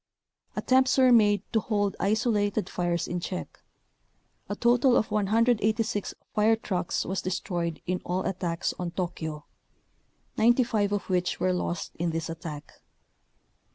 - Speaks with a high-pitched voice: Yes, high, 200 Hz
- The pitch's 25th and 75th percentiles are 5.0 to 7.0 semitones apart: No, average, 3.9 semitones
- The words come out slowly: Yes, slow, 130 wpm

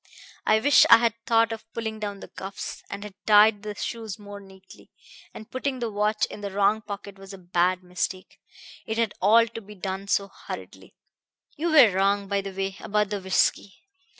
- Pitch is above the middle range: Yes, high, 205 Hz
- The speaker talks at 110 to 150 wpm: No, average, 195 wpm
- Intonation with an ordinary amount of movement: No, narrow, 2.2 semitones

